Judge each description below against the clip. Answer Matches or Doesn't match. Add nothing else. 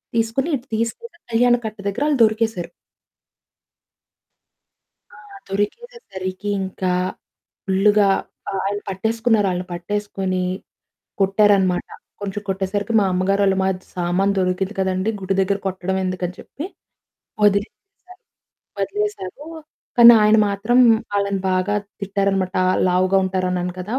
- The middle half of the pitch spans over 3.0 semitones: Doesn't match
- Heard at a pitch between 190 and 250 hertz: Matches